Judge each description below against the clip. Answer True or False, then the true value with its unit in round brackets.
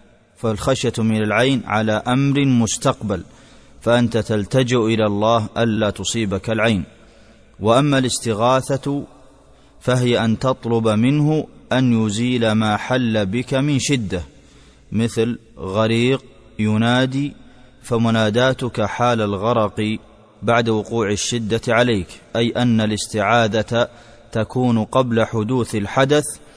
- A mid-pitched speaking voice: False (115 Hz)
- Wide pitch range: False (2.6 semitones)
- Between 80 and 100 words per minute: True (95 wpm)